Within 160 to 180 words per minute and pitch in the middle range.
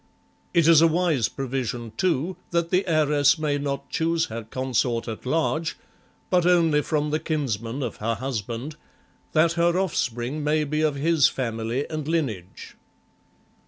No: average, 150 wpm; medium, 150 Hz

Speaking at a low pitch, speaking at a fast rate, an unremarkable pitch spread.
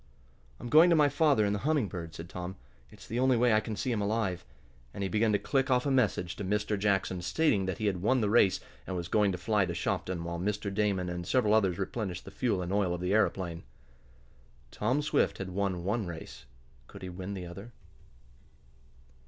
Yes: low, 100 Hz; fast, 220 wpm; average, 3.7 semitones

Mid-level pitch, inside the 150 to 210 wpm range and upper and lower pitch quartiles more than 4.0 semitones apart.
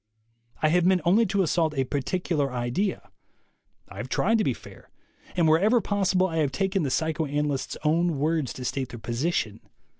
Yes: medium, 160 Hz; average, 175 wpm; average, 5.0 semitones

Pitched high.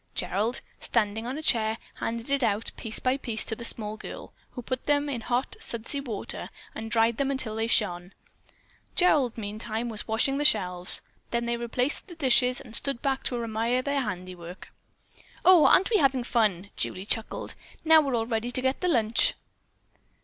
Yes: high, 235 Hz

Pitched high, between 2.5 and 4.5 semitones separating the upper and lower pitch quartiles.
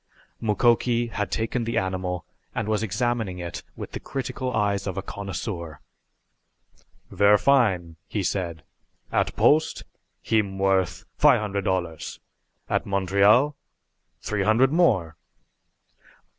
No: low, 100 Hz; average, 3.8 semitones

